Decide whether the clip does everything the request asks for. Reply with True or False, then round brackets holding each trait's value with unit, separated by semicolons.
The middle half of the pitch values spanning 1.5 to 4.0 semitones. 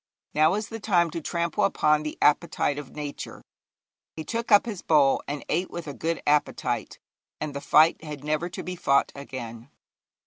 True (2.9 semitones)